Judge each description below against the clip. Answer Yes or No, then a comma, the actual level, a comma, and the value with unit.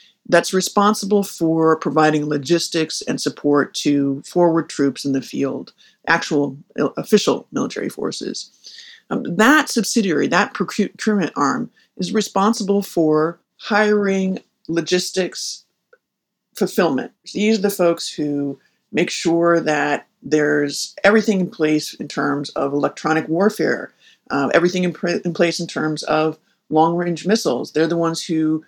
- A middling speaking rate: No, slow, 130 wpm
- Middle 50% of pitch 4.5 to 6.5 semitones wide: Yes, average, 4.8 semitones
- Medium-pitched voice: Yes, medium, 170 Hz